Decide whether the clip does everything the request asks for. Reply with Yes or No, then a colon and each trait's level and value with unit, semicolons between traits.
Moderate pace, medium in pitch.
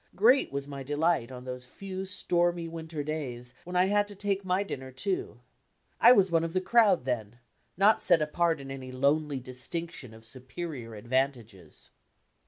Yes: average, 170 wpm; medium, 150 Hz